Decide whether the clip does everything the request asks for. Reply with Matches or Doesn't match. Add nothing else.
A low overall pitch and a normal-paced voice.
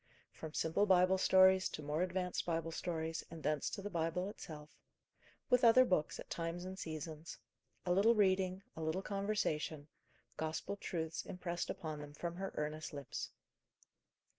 Doesn't match